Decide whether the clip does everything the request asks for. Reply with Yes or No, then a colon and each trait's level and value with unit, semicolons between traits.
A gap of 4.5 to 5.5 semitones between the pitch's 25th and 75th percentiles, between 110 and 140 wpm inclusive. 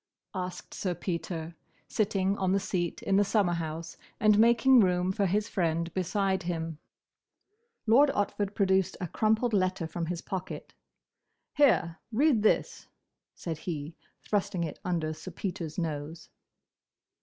No: average, 3.4 semitones; slow, 135 wpm